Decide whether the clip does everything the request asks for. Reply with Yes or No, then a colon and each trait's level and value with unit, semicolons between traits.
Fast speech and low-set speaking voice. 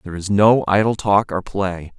Yes: fast, 210 wpm; low, 100 Hz